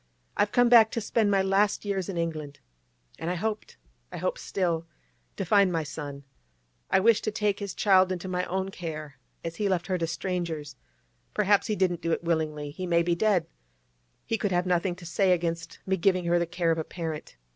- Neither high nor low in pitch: Yes, medium, 175 Hz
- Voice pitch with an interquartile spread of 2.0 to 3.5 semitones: Yes, average, 3.2 semitones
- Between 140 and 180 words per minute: No, average, 195 wpm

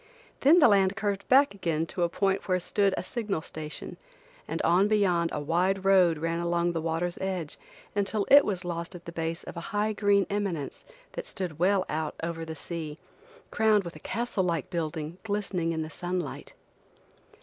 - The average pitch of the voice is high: No, medium, 180 Hz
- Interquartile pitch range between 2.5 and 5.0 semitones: Yes, average, 3.4 semitones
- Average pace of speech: Yes, average, 185 wpm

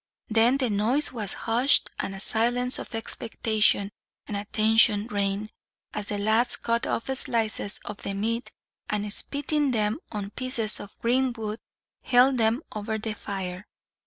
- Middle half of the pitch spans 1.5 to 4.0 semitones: Yes, narrow, 2.6 semitones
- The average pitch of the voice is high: Yes, high, 220 Hz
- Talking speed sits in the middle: Yes, average, 150 wpm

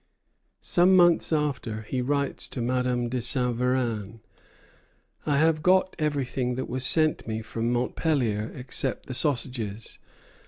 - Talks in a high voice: No, low, 125 Hz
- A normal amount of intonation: Yes, average, 3.7 semitones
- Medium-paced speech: No, slow, 130 wpm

